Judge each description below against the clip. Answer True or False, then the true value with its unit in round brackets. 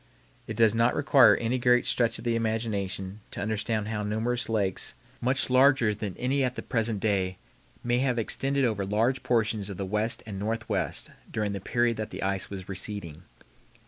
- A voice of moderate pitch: False (110 Hz)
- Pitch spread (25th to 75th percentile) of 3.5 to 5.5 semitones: False (3.1 semitones)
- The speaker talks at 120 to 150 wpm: False (180 wpm)